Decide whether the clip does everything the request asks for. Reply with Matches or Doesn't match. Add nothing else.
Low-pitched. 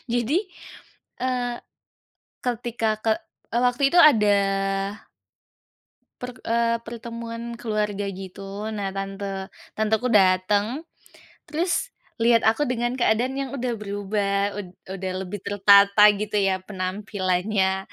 Doesn't match